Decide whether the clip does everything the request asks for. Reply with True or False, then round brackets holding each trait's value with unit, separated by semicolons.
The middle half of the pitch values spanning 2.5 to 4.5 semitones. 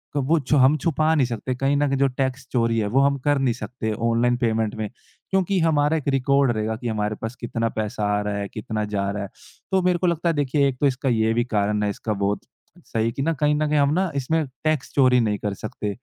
False (4.9 semitones)